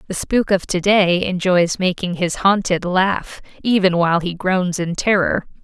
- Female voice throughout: Yes, female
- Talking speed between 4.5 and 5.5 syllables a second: No, 4.3 syllables/s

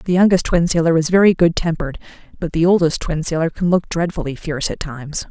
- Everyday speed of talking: No, fast, 215 wpm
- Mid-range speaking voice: Yes, medium, 165 Hz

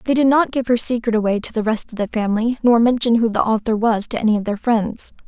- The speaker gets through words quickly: Yes, fast, 275 wpm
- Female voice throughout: Yes, female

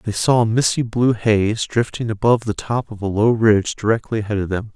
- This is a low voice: Yes, low, 110 Hz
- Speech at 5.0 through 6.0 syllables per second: Yes, 5.5 syllables/s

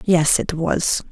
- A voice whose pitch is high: No, medium, 170 Hz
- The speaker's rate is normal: Yes, average, 160 wpm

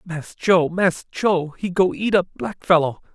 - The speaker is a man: Yes, male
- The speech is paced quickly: No, average, 190 wpm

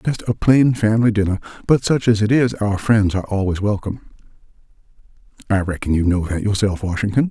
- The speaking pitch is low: Yes, low, 105 Hz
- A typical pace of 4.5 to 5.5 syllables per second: No, 6.0 syllables/s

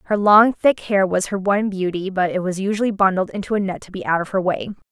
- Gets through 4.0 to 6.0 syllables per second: No, 6.2 syllables/s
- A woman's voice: Yes, female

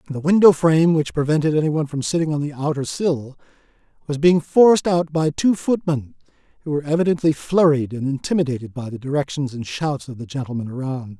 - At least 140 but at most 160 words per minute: No, average, 180 wpm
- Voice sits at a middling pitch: Yes, medium, 145 Hz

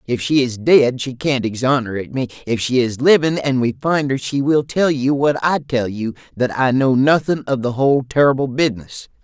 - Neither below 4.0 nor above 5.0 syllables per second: No, 5.2 syllables/s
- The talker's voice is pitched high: No, low, 130 Hz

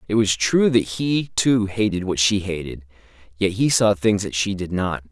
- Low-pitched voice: Yes, low, 100 Hz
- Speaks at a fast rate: Yes, fast, 210 wpm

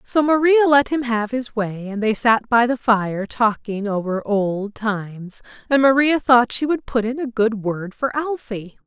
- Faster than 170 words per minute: Yes, average, 195 wpm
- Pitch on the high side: Yes, high, 235 Hz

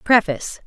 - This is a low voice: No, high, 195 Hz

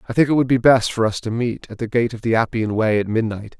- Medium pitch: No, low, 115 Hz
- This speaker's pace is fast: Yes, fast, 315 wpm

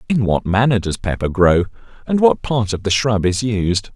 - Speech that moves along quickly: Yes, fast, 210 wpm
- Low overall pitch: Yes, low, 105 Hz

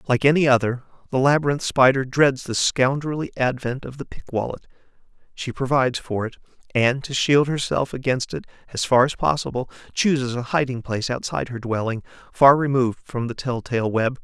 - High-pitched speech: No, low, 130 Hz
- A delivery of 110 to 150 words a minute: No, average, 175 wpm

